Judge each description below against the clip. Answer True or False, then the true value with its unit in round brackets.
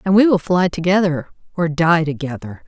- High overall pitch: False (170 Hz)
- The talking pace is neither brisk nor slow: True (180 wpm)